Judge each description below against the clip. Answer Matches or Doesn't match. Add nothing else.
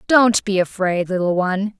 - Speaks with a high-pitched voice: Matches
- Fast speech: Doesn't match